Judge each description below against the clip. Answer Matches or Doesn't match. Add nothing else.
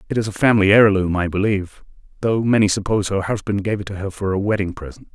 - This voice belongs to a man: Matches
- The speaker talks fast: Matches